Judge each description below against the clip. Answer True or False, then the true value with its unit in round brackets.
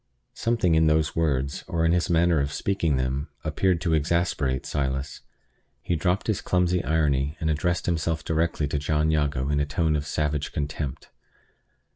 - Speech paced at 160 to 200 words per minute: True (165 wpm)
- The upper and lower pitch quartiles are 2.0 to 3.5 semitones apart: True (2.7 semitones)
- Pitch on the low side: True (80 Hz)